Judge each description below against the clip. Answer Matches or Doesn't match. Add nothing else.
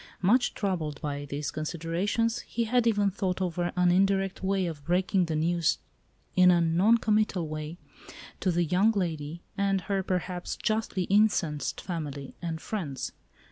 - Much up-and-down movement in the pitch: Doesn't match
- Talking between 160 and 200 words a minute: Doesn't match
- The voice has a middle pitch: Matches